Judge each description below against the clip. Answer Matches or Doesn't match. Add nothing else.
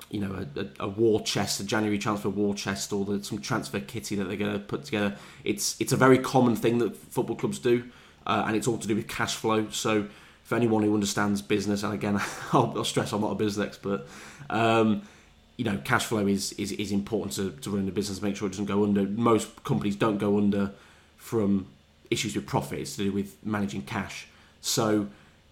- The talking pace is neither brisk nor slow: Doesn't match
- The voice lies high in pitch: Doesn't match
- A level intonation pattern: Matches